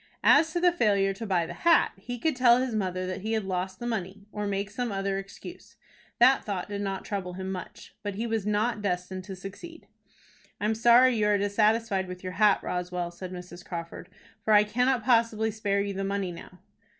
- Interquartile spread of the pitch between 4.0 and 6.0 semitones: No, average, 3.2 semitones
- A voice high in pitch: Yes, high, 200 Hz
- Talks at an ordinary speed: No, fast, 210 wpm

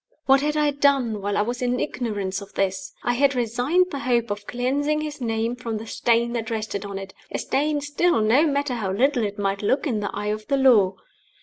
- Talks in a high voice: Yes, high, 240 Hz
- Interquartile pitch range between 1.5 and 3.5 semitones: No, average, 5.1 semitones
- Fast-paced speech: Yes, fast, 225 wpm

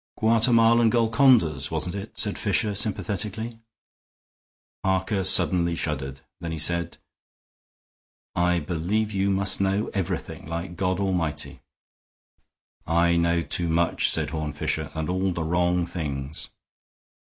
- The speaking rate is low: Yes, slow, 120 wpm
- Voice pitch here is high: No, very low, 90 Hz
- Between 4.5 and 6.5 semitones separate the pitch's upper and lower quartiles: No, average, 3.5 semitones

